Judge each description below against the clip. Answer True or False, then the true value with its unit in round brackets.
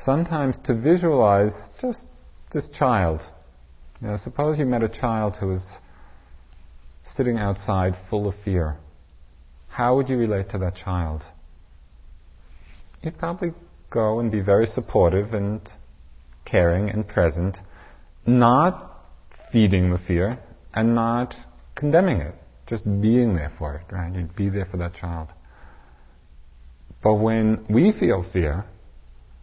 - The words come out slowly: True (130 wpm)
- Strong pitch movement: True (7.0 semitones)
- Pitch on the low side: True (95 Hz)